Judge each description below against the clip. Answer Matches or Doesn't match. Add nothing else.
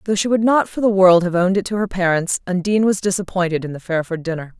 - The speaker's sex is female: Matches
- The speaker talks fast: Matches